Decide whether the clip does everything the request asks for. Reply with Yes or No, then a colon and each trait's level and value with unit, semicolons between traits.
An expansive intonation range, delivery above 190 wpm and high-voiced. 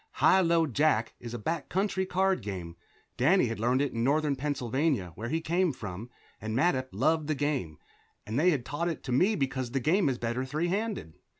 No: wide, 5.9 semitones; fast, 205 wpm; medium, 140 Hz